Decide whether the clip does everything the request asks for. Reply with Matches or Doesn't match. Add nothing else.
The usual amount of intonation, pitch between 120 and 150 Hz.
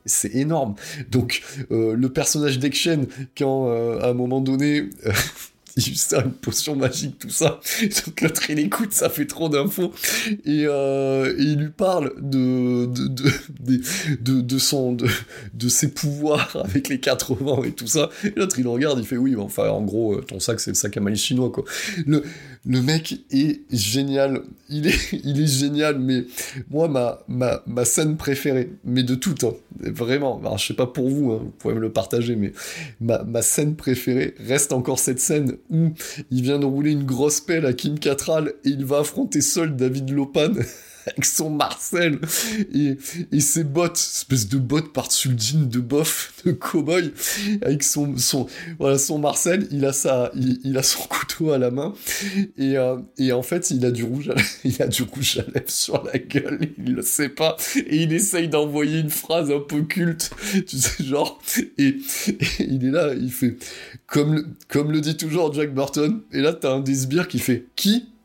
Matches